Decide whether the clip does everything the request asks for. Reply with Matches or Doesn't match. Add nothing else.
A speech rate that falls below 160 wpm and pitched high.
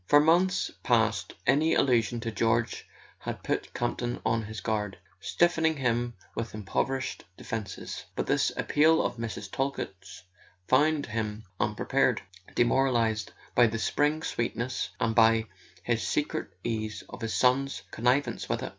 Doesn't match